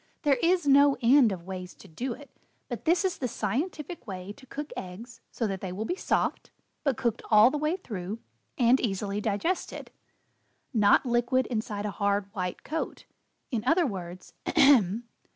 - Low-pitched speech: No, high, 230 Hz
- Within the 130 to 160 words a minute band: No, average, 170 wpm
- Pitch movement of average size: No, wide, 6.0 semitones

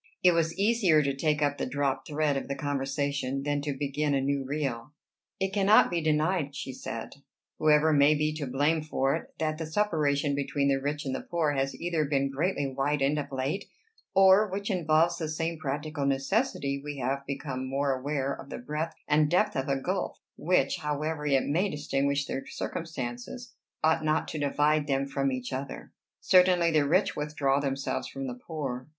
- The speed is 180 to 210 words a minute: Yes, average, 185 wpm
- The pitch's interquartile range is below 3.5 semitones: Yes, narrow, 2.6 semitones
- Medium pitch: Yes, medium, 145 Hz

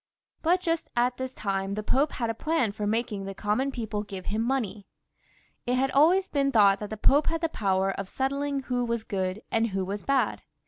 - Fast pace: Yes, fast, 215 wpm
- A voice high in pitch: Yes, high, 230 Hz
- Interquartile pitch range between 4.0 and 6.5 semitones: Yes, average, 5.1 semitones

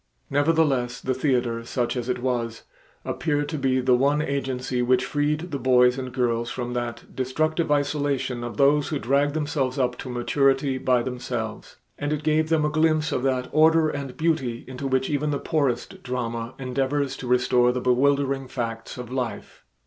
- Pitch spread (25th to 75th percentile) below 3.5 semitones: Yes, average, 2.7 semitones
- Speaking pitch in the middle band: No, low, 130 Hz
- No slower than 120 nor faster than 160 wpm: No, average, 175 wpm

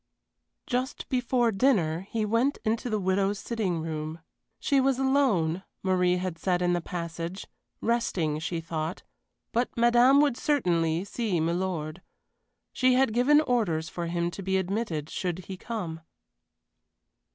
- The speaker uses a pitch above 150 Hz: Yes, high, 190 Hz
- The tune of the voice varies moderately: No, wide, 6.0 semitones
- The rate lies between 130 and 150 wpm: Yes, average, 140 wpm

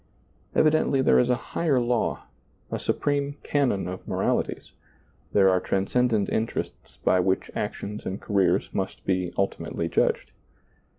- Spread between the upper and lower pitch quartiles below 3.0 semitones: No, wide, 5.5 semitones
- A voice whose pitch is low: Yes, low, 105 Hz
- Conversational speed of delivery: No, slow, 130 wpm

